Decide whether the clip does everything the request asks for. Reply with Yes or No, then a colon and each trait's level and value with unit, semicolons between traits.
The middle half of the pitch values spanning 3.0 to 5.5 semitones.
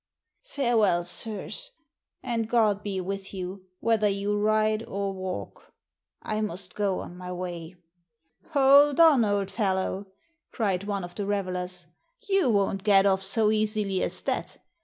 No: narrow, 2.4 semitones